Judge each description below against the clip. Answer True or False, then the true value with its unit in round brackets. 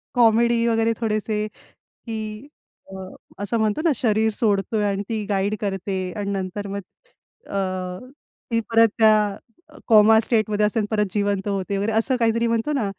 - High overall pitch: True (215 Hz)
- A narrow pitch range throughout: True (2.0 semitones)